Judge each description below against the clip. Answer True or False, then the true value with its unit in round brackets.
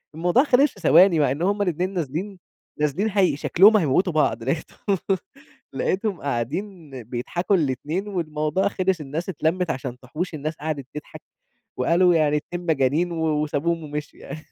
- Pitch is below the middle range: False (165 Hz)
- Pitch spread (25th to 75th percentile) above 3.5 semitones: True (4.0 semitones)